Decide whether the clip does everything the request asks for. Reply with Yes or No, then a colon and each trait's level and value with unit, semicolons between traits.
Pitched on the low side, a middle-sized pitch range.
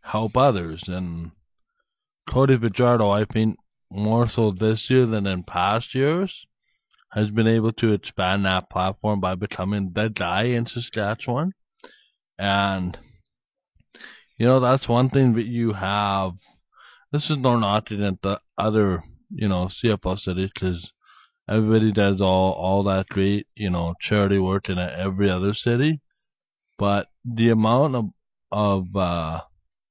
Yes: low, 105 Hz; average, 3.7 semitones